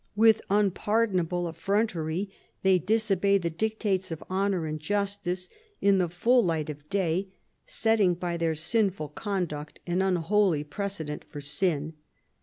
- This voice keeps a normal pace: No, slow, 130 wpm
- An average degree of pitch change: Yes, average, 3.7 semitones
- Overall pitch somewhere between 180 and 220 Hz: Yes, medium, 185 Hz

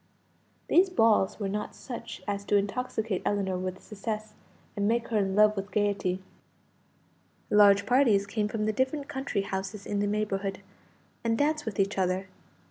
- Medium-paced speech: Yes, average, 160 wpm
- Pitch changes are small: Yes, narrow, 2.3 semitones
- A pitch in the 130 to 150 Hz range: No, high, 205 Hz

